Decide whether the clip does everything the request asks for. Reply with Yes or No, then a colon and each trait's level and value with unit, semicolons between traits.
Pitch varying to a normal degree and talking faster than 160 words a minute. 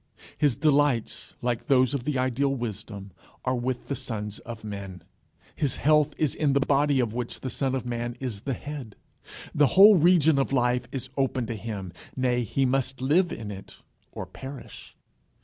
Yes: average, 3.1 semitones; average, 180 wpm